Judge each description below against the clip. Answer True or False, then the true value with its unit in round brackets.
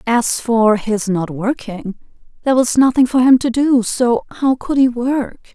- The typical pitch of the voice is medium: False (240 Hz)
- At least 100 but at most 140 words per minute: False (175 wpm)